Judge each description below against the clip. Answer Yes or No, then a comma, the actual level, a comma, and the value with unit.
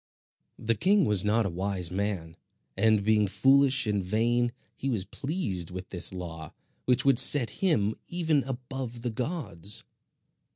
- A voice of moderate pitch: No, low, 110 Hz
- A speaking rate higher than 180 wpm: No, average, 150 wpm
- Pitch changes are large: Yes, wide, 5.7 semitones